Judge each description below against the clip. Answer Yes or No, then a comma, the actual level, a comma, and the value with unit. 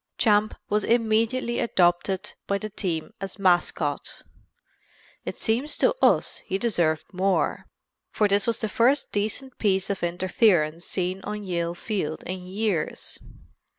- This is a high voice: Yes, high, 200 Hz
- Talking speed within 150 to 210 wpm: No, slow, 135 wpm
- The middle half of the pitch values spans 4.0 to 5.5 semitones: No, average, 3.5 semitones